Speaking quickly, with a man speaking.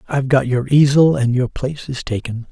Yes: fast, 215 wpm; male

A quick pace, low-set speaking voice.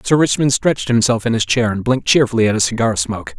Yes: fast, 250 wpm; low, 115 Hz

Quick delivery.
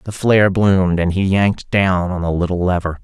Yes: fast, 215 wpm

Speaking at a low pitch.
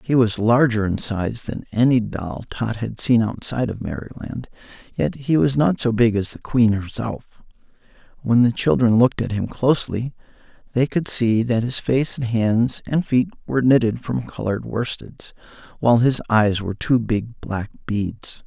Yes: low, 115 Hz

